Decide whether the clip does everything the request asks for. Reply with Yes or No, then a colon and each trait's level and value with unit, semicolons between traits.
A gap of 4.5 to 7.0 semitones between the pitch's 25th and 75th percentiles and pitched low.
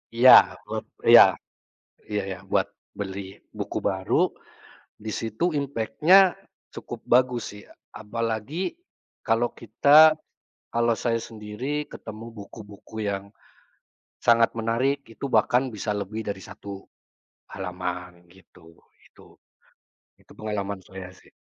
No: average, 3.4 semitones; low, 110 Hz